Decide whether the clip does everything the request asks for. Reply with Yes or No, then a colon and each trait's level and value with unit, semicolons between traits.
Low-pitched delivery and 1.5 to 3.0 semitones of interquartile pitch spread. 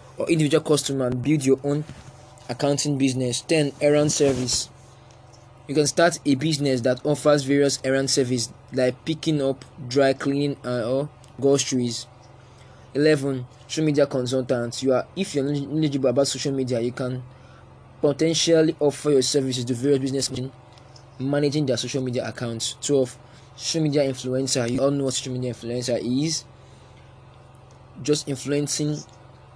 Yes: low, 130 Hz; narrow, 2.4 semitones